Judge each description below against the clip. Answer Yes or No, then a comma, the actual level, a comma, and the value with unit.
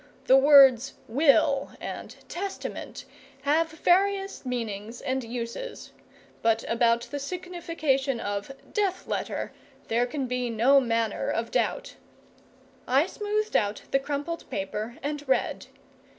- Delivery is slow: Yes, slow, 120 wpm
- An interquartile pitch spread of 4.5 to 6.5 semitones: Yes, wide, 5.6 semitones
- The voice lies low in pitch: No, very high, 270 Hz